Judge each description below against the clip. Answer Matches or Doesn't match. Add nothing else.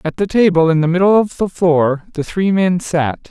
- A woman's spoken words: Doesn't match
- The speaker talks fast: Matches